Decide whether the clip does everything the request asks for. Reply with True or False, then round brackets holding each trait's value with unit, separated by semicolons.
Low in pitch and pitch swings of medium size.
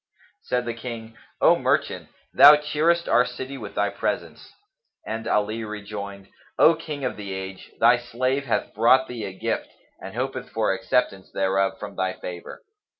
True (115 Hz; 4.6 semitones)